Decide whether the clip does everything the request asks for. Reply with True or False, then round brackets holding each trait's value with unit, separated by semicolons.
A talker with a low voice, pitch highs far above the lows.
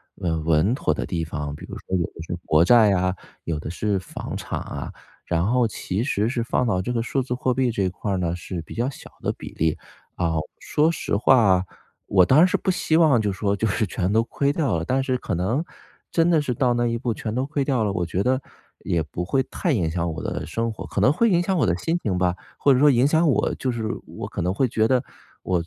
True (110 Hz; 6.5 semitones)